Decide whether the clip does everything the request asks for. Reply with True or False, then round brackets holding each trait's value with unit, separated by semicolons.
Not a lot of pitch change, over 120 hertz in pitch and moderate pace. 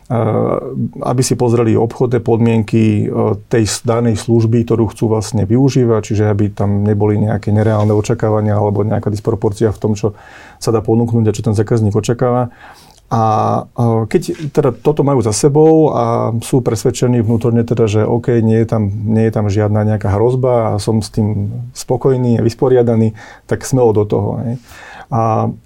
False (2.0 semitones; 115 Hz; 155 wpm)